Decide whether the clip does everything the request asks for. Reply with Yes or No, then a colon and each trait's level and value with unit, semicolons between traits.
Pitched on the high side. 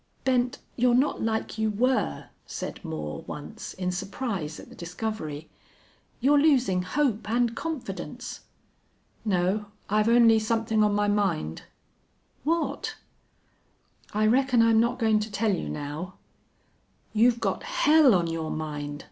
Yes: high, 215 Hz